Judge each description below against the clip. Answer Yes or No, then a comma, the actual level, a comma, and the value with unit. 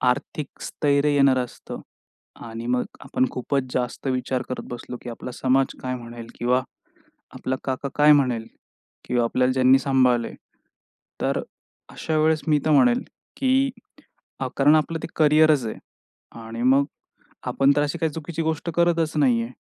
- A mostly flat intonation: No, average, 3.5 semitones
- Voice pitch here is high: No, low, 135 Hz